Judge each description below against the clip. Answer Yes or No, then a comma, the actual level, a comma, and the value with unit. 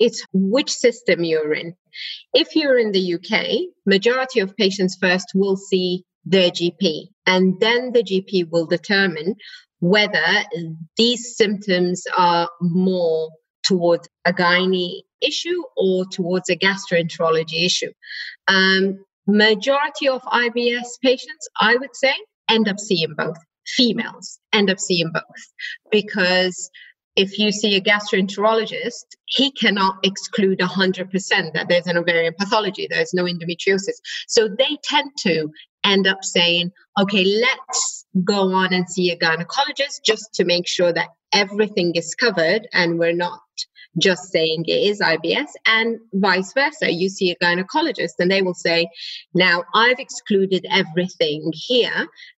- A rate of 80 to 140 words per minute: Yes, slow, 135 wpm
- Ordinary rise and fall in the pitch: Yes, average, 4.7 semitones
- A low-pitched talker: No, high, 195 Hz